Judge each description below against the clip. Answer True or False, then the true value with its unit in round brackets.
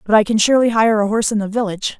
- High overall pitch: True (215 Hz)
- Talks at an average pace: False (300 wpm)